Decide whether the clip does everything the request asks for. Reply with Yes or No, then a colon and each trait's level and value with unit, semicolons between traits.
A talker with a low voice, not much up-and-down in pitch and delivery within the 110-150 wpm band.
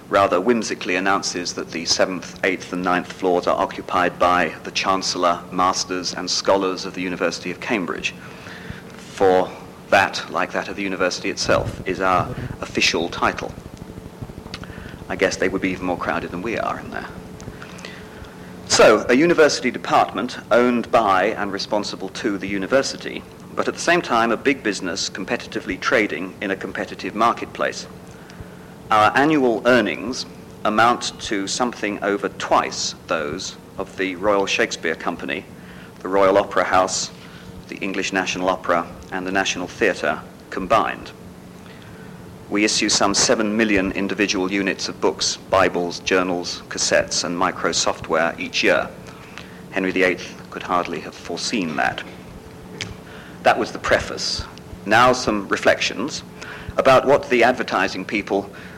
Yes: very low, 95 Hz; narrow, 2.0 semitones; average, 140 wpm